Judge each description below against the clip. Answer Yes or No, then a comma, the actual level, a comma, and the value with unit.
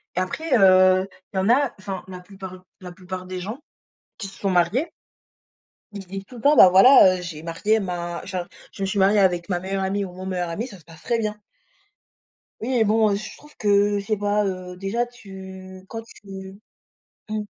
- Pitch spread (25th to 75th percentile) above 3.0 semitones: No, narrow, 2.4 semitones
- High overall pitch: Yes, high, 195 Hz